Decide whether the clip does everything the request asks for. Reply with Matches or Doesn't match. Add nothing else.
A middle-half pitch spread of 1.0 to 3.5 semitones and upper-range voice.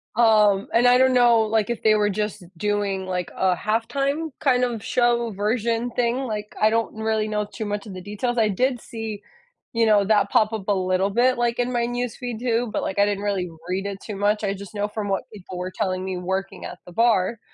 Matches